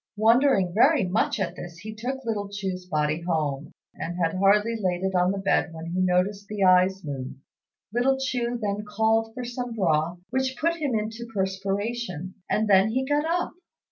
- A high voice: Yes, high, 200 Hz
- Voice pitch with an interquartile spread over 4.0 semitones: Yes, average, 4.6 semitones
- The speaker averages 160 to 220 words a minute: Yes, average, 185 wpm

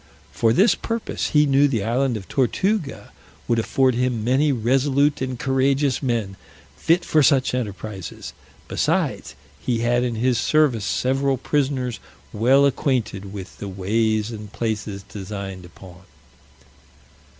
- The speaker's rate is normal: No, slow, 130 wpm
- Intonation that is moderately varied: Yes, average, 4.2 semitones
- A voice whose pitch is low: Yes, low, 125 Hz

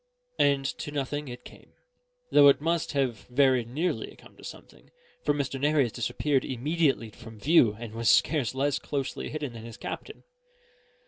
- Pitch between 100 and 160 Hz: Yes, low, 135 Hz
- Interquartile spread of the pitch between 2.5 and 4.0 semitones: Yes, average, 3.6 semitones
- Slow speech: No, average, 160 wpm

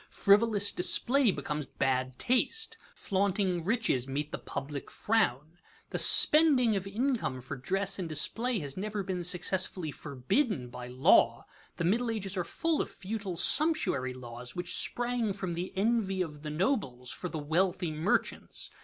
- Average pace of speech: Yes, average, 150 wpm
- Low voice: No, medium, 185 Hz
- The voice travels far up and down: Yes, wide, 6.7 semitones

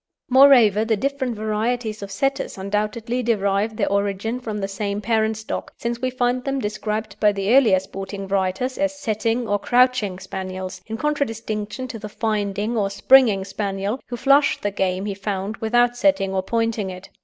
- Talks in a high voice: Yes, high, 215 Hz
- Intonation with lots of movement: No, average, 3.5 semitones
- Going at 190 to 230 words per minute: No, average, 170 wpm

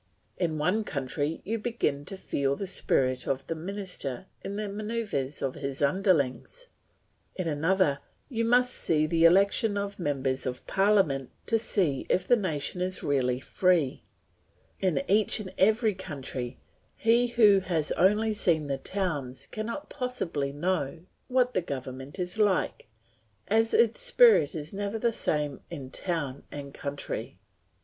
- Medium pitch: Yes, medium, 180 Hz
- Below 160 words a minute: Yes, average, 145 wpm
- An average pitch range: No, wide, 6.8 semitones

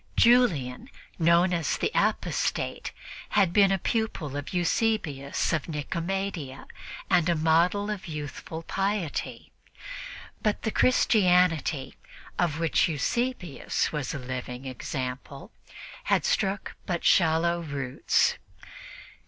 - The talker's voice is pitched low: No, medium, 170 Hz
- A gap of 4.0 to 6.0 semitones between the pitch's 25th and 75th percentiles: Yes, average, 5.1 semitones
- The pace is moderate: No, slow, 105 wpm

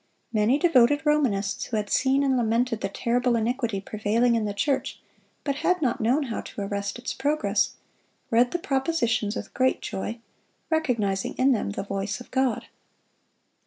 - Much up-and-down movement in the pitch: No, average, 4.3 semitones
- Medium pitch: No, high, 240 Hz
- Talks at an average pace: Yes, average, 160 wpm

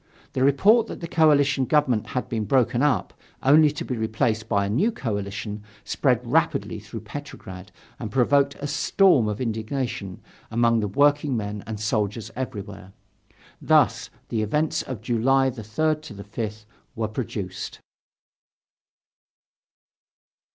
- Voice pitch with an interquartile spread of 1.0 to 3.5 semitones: No, average, 4.8 semitones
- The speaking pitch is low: Yes, low, 115 Hz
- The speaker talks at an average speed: No, slow, 125 wpm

